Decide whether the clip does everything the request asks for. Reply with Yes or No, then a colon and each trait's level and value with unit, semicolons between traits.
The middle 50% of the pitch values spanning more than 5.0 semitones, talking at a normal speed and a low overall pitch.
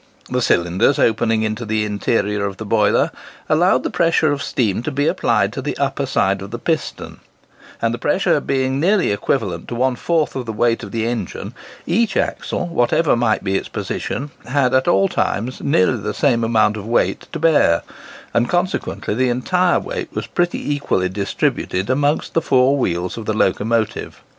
Yes: wide, 5.5 semitones; average, 180 wpm; low, 120 Hz